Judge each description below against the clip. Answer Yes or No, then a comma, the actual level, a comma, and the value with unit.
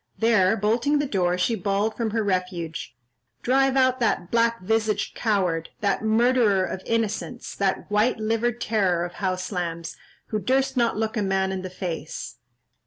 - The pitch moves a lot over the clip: No, average, 3.9 semitones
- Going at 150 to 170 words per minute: Yes, average, 165 wpm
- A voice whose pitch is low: No, high, 210 Hz